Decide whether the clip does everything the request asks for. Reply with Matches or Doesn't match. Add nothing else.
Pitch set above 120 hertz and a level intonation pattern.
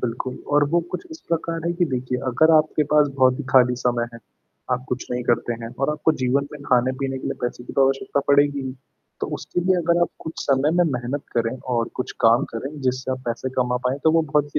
Doesn't match